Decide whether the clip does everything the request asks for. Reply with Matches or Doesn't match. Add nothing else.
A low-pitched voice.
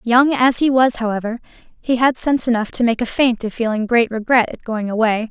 Doesn't match